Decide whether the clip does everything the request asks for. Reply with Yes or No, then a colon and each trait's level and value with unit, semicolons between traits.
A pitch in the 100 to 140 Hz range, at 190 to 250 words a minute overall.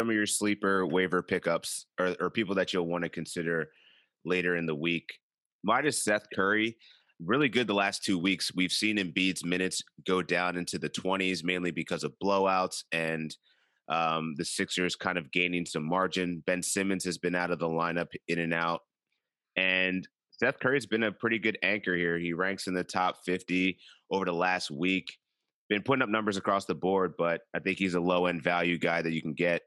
No: very low, 90 Hz; average, 200 wpm